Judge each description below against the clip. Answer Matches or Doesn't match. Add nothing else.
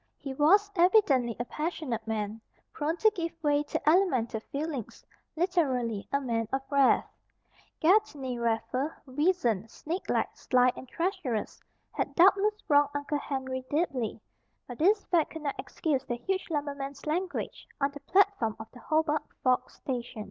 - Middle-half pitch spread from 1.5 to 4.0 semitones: Doesn't match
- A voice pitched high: Matches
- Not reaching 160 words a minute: Matches